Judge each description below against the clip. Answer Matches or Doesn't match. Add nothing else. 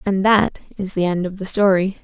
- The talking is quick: Matches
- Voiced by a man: Doesn't match